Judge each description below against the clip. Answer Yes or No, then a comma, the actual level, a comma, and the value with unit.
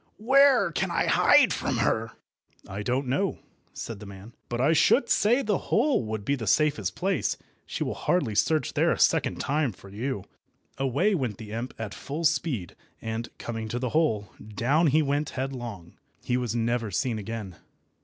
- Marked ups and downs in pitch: Yes, wide, 6.1 semitones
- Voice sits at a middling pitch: No, low, 125 Hz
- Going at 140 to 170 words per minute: No, average, 180 wpm